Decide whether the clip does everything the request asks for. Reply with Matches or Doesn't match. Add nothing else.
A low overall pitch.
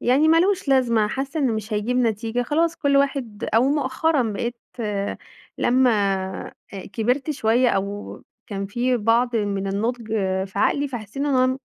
Doesn't match